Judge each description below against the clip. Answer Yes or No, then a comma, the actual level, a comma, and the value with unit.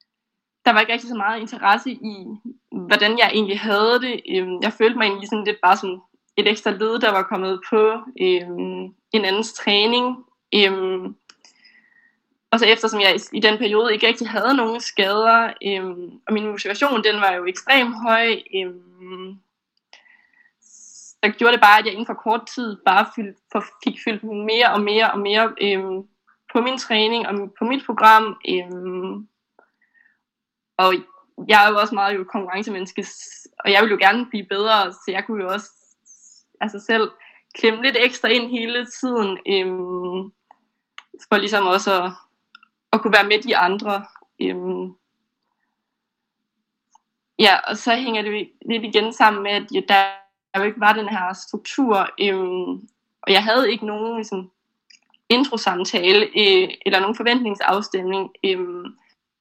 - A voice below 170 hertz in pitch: No, high, 215 Hz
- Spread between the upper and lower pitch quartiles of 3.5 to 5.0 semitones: No, average, 3.1 semitones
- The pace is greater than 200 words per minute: No, average, 155 wpm